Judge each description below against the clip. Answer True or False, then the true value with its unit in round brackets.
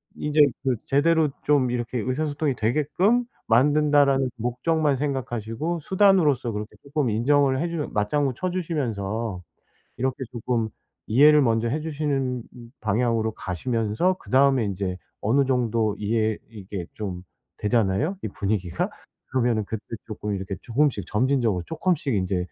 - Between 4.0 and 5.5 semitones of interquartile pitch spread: True (5.2 semitones)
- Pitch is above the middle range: False (125 Hz)